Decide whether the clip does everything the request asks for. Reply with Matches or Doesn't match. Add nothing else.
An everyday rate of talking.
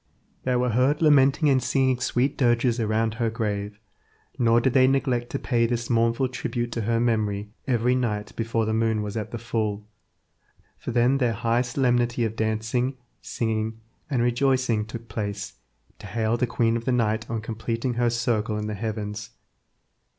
Matches